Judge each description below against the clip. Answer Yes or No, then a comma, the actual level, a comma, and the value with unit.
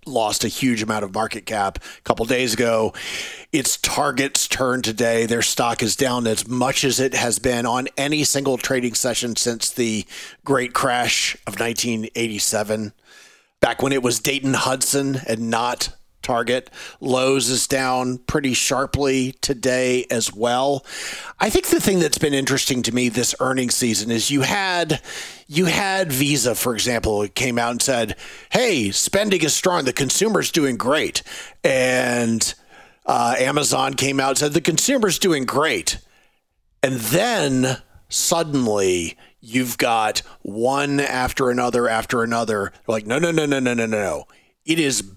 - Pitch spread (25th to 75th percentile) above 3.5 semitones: No, average, 3.1 semitones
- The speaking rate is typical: Yes, average, 155 wpm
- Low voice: Yes, low, 125 Hz